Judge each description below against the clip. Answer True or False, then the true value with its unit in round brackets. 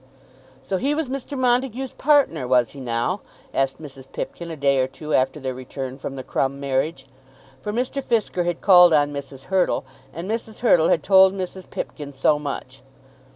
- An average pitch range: False (7.2 semitones)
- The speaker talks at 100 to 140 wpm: False (180 wpm)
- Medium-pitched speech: True (155 Hz)